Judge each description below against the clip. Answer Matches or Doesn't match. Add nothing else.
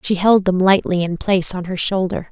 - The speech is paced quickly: Matches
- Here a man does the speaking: Doesn't match